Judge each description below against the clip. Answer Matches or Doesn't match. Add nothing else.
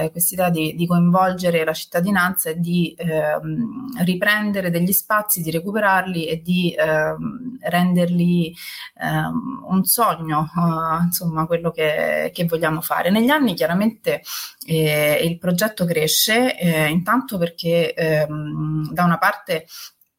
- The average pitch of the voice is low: Doesn't match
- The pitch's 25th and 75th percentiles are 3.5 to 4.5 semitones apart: Doesn't match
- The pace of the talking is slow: Doesn't match